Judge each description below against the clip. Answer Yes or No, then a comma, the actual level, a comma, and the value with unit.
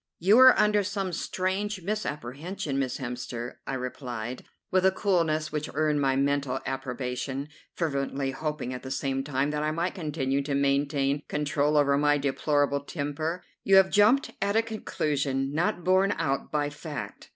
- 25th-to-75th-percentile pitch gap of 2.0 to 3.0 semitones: No, average, 4.6 semitones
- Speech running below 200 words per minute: Yes, average, 160 wpm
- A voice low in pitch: No, medium, 145 Hz